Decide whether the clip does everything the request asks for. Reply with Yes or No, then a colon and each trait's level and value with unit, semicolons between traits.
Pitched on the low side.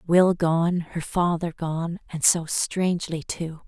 No: medium, 170 Hz